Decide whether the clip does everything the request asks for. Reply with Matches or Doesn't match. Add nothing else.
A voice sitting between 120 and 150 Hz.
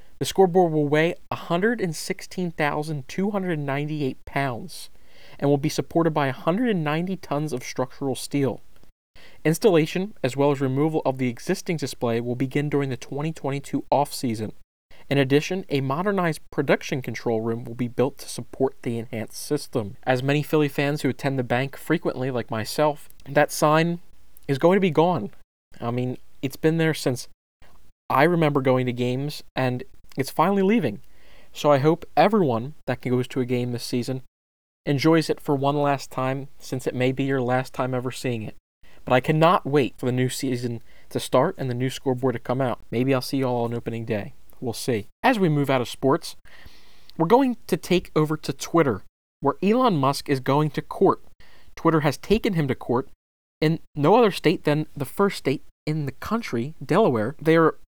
Matches